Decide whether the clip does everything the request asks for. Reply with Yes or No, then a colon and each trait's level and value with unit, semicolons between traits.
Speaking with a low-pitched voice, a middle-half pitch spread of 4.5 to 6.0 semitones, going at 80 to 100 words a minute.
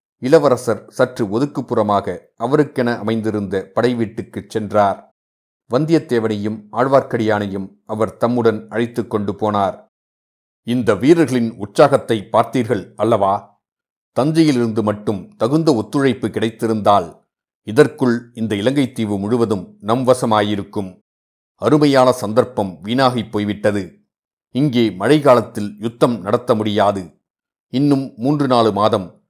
No: low, 115 Hz; average, 3.3 semitones; average, 90 wpm